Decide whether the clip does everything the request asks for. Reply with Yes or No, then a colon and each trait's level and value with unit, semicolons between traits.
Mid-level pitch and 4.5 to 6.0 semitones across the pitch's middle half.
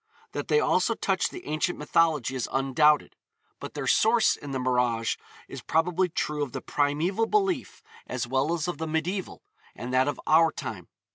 Yes: medium, 150 Hz; average, 5.0 semitones